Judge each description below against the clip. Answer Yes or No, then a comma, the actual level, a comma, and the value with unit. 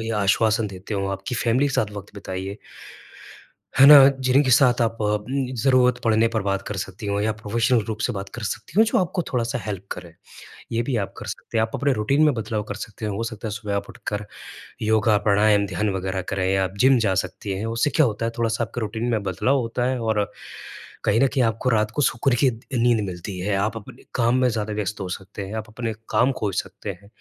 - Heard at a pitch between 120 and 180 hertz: No, low, 110 Hz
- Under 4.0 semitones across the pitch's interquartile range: Yes, average, 2.8 semitones